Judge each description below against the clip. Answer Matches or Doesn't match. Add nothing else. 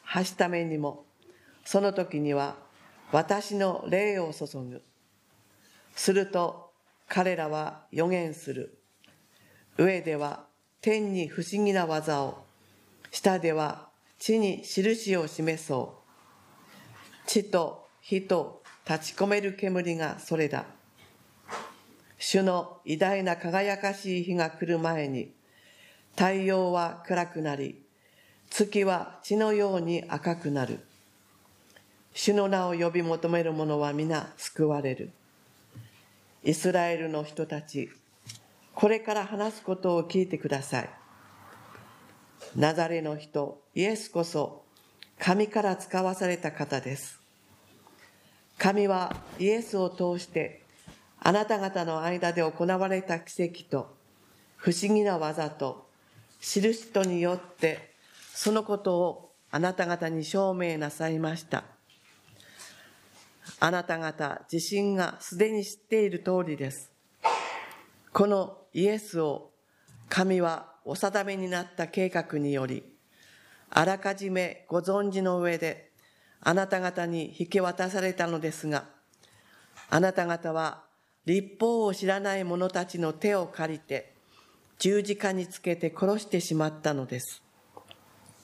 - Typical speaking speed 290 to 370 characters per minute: Doesn't match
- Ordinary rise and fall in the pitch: Matches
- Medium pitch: Matches